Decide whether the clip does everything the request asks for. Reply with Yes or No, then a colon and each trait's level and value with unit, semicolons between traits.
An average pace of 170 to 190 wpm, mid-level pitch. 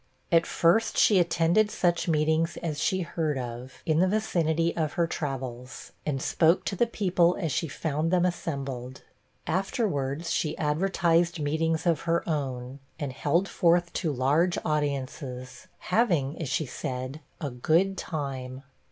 No: average, 145 wpm; medium, 160 Hz